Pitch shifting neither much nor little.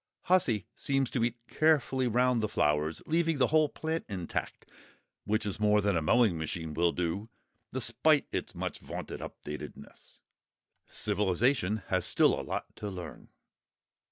No: wide, 6.6 semitones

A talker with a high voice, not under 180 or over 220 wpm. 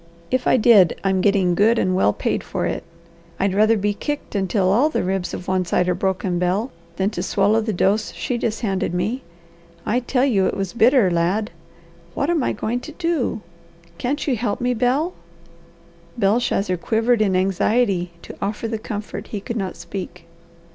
Yes: high, 210 Hz; average, 185 wpm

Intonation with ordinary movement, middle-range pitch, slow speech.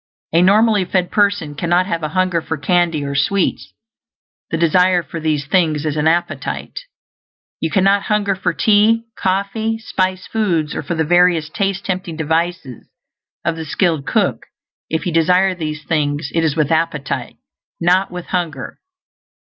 No: average, 3.1 semitones; medium, 175 Hz; average, 155 wpm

